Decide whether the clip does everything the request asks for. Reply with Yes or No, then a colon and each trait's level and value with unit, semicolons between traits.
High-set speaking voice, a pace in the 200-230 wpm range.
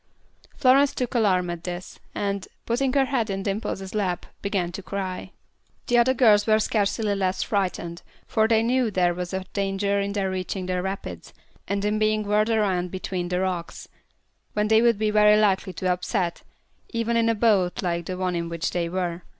No: high, 200 Hz; average, 190 wpm